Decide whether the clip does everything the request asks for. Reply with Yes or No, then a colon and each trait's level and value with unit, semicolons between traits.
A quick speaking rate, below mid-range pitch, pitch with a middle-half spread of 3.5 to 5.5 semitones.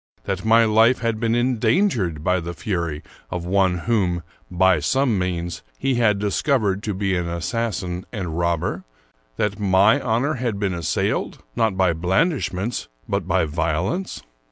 No: average, 155 wpm; very low, 95 Hz; average, 4.7 semitones